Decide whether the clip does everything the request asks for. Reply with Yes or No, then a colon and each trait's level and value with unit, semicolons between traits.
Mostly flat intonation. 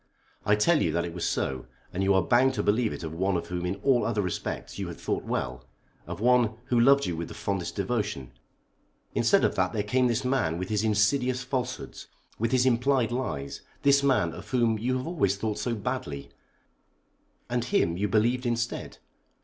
No: average, 5.2 semitones